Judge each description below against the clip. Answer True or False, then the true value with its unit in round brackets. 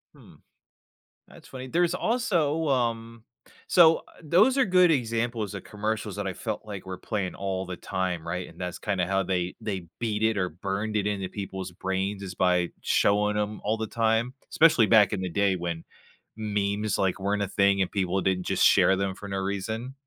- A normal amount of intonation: True (3.1 semitones)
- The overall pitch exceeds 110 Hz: False (100 Hz)